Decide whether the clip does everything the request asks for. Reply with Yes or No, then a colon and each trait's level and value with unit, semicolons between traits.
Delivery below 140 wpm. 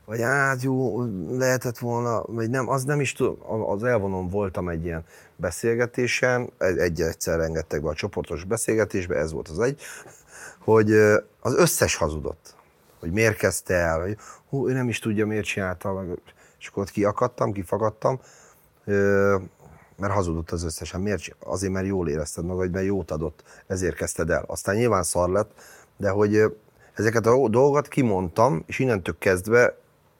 No: average, 150 wpm